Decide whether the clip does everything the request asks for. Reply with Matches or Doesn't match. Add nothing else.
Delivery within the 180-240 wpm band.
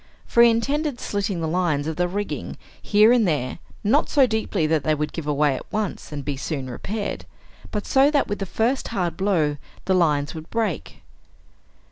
Matches